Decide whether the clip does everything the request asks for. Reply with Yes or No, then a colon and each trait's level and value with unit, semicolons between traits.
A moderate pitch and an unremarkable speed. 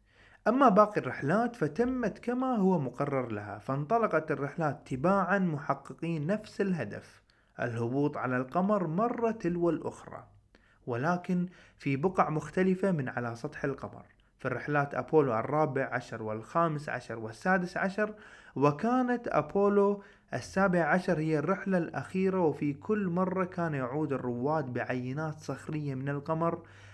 Yes: medium, 155 Hz; average, 120 wpm